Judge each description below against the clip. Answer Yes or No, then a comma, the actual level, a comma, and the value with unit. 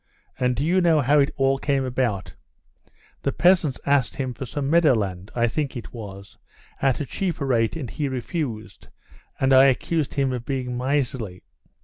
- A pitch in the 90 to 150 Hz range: Yes, low, 135 Hz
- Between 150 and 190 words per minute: Yes, average, 170 wpm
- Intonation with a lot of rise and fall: No, average, 3.1 semitones